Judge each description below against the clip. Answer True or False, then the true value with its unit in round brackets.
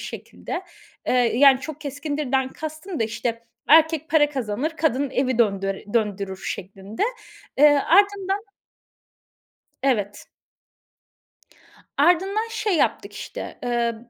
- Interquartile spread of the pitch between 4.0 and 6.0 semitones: True (5.6 semitones)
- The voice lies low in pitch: False (275 Hz)